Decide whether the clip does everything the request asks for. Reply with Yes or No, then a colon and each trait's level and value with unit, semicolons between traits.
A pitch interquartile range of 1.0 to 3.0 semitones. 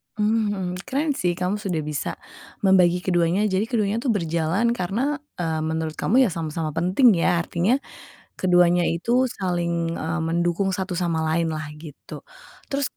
No: average, 3.9 semitones